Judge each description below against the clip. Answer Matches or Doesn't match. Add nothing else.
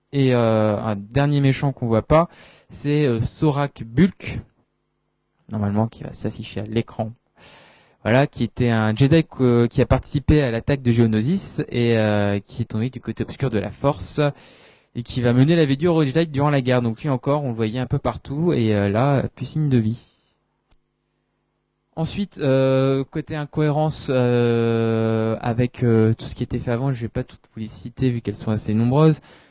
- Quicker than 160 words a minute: Matches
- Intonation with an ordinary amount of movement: Matches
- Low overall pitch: Matches